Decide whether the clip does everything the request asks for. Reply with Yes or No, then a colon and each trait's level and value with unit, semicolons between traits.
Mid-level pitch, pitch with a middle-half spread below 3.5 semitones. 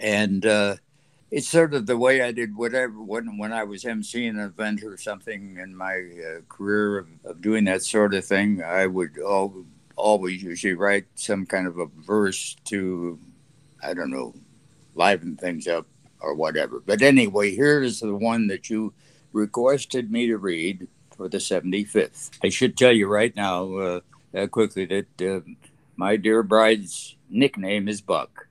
No: low, 105 Hz; average, 3.1 semitones